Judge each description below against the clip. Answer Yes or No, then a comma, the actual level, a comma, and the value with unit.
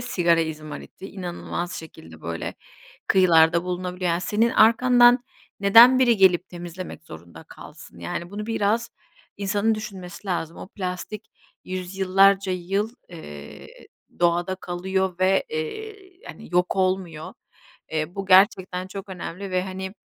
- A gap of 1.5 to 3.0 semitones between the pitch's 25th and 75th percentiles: Yes, narrow, 2.5 semitones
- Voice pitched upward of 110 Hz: Yes, medium, 185 Hz